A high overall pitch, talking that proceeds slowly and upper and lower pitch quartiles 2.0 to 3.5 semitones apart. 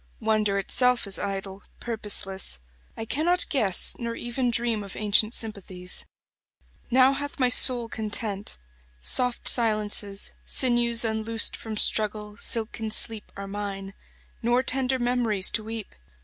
Yes: high, 220 Hz; slow, 130 wpm; average, 2.8 semitones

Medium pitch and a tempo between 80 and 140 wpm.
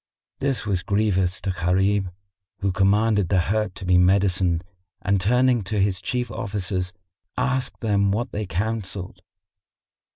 No: low, 100 Hz; slow, 135 wpm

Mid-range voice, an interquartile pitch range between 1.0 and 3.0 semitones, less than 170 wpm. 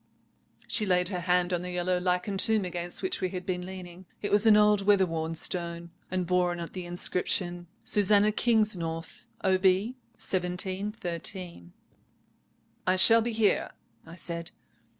Yes: medium, 180 Hz; narrow, 2.5 semitones; average, 150 wpm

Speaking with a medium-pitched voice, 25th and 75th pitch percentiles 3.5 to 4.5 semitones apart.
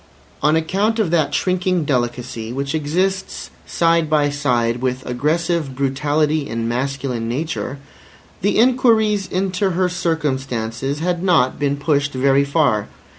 No: medium, 145 Hz; average, 4.9 semitones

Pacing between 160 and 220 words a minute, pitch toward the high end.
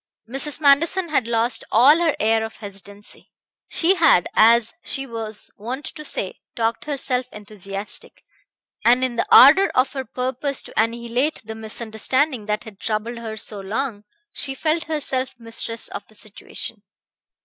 No: average, 150 wpm; high, 235 Hz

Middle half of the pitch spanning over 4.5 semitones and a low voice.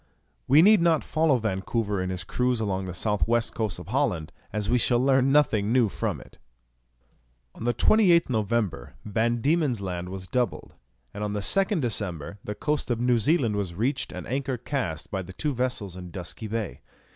Yes: average, 5.3 semitones; low, 115 Hz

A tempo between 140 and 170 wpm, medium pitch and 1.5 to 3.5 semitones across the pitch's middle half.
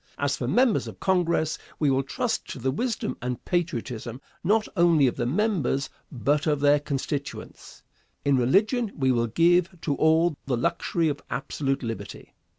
No: average, 160 wpm; medium, 145 Hz; average, 4.8 semitones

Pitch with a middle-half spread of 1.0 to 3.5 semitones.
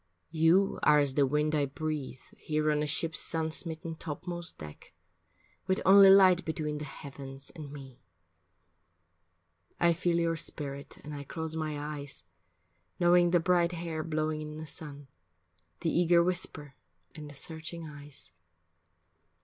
Yes: narrow, 2.6 semitones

